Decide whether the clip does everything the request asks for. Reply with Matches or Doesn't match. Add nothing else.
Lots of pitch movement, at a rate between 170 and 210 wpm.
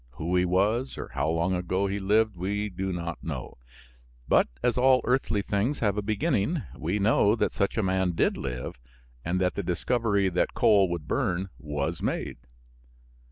Doesn't match